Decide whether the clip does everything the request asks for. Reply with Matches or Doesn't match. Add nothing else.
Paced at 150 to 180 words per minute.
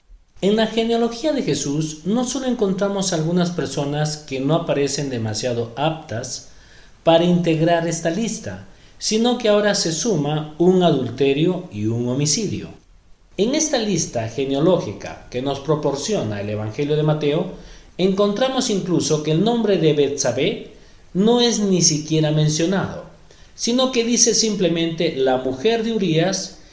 Doesn't match